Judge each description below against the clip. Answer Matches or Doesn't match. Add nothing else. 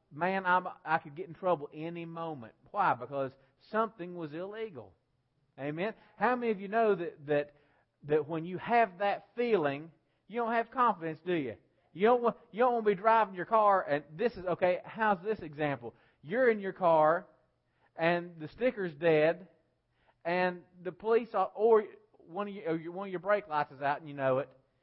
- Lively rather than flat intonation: Matches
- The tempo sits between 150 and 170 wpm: Doesn't match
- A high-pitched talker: Doesn't match